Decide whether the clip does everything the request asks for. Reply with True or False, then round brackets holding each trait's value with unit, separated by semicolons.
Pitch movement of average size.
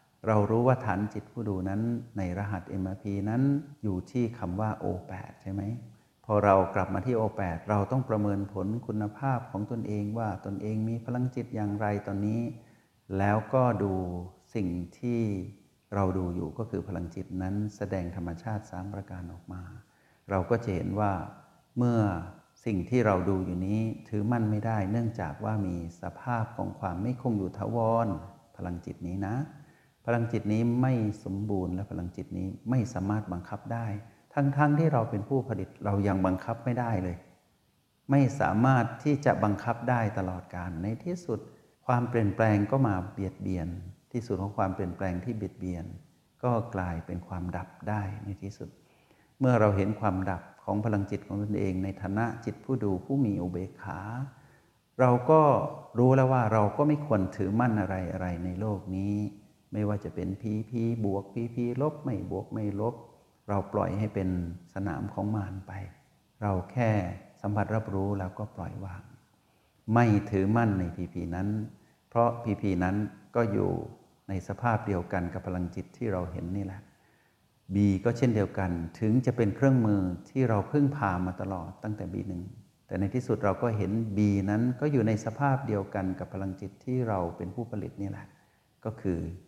True (3.5 semitones)